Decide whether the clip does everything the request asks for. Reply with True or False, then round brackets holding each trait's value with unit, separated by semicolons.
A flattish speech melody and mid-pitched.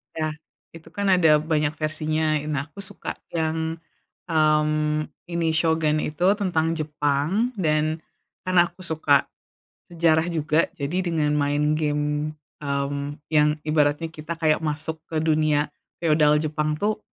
True (1.4 semitones; 155 Hz)